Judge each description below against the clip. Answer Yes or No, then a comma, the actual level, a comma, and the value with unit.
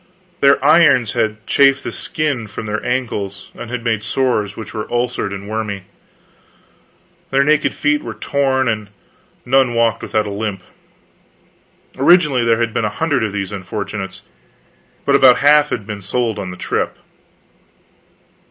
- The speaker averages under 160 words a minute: Yes, average, 150 wpm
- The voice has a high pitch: No, low, 115 Hz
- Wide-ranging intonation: No, average, 4.4 semitones